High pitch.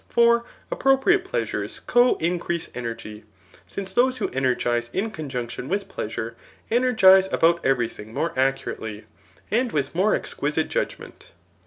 No: medium, 170 Hz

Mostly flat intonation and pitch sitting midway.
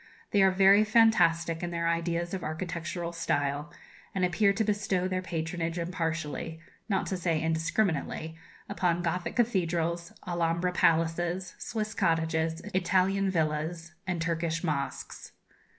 Yes: narrow, 2.2 semitones; medium, 170 Hz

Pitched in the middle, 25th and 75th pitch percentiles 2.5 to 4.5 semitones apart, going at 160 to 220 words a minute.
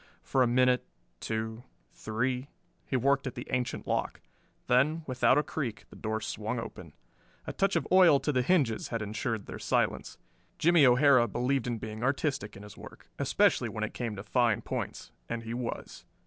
No: low, 125 Hz; average, 3.5 semitones; average, 180 wpm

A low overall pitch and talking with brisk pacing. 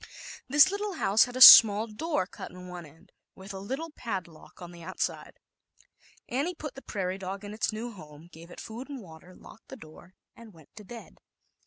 No: high, 200 Hz; fast, 210 wpm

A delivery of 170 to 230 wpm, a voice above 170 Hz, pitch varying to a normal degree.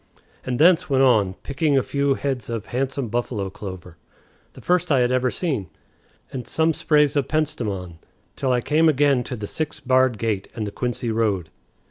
No: average, 180 wpm; low, 130 Hz; average, 4.9 semitones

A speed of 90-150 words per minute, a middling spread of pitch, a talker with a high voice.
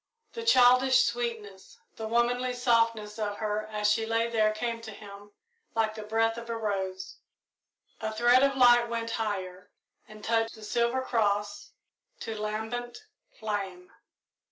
No: average, 145 wpm; narrow, 2.1 semitones; high, 225 Hz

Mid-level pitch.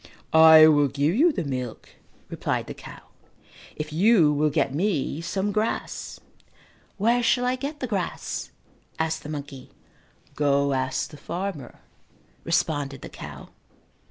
Yes: medium, 155 Hz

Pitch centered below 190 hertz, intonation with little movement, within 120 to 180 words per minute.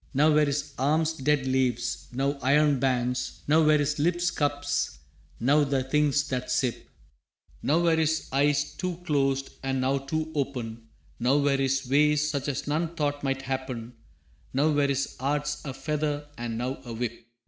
Yes: medium, 140 Hz; narrow, 2.2 semitones; average, 170 wpm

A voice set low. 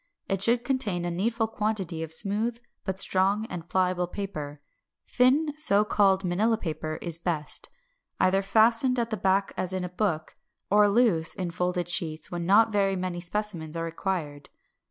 No: high, 190 Hz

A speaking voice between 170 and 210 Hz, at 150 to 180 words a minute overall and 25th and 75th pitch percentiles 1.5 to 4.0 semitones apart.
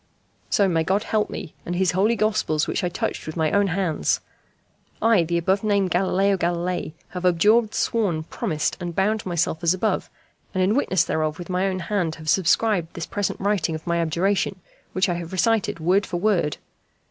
No: medium, 185 Hz; average, 190 wpm; average, 3.1 semitones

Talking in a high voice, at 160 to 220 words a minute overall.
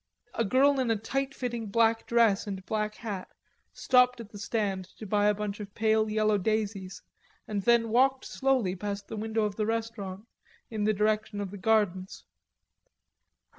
Yes: high, 215 Hz; average, 170 wpm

